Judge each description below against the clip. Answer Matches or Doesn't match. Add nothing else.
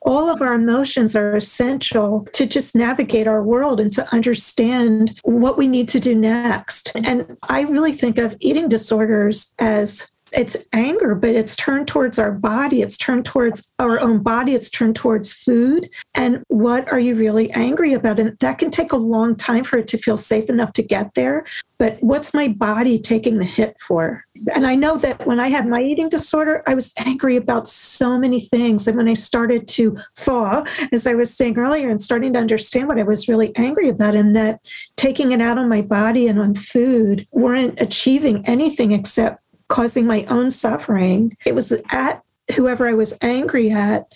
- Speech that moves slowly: Doesn't match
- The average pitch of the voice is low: Doesn't match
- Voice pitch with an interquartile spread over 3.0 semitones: Doesn't match